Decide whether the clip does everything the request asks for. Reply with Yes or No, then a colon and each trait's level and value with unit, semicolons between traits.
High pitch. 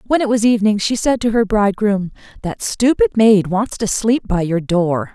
Yes: high, 210 Hz